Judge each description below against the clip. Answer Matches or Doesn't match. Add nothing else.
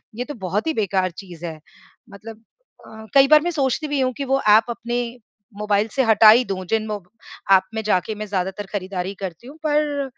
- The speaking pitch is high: Matches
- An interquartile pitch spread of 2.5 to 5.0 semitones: Doesn't match